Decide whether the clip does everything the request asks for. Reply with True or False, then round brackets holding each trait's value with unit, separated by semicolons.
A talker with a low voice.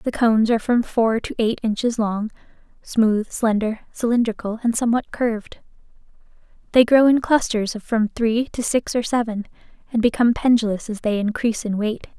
False (225 Hz)